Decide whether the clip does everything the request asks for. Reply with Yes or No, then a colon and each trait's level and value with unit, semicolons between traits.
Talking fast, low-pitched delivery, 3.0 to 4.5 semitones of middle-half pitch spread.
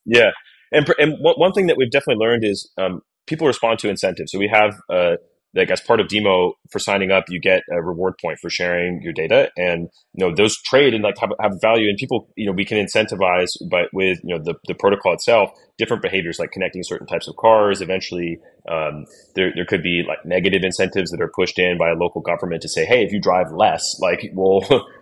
Yes: fast, 230 wpm; very low, 95 Hz; average, 4.0 semitones